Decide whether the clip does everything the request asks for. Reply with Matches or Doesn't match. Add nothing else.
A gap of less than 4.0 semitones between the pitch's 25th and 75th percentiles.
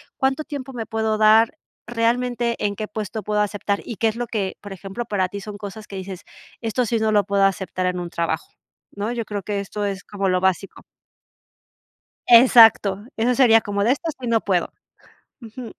Matches